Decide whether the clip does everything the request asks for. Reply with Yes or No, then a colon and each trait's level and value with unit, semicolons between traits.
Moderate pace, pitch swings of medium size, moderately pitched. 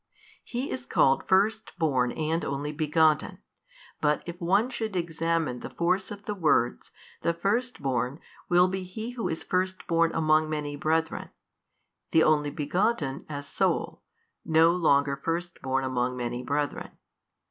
Yes: average, 145 wpm; average, 4.2 semitones; medium, 160 Hz